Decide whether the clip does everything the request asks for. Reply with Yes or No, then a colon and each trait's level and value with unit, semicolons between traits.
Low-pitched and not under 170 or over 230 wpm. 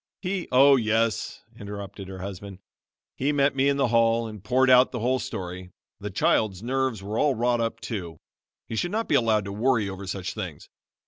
Yes: low, 115 Hz; average, 200 wpm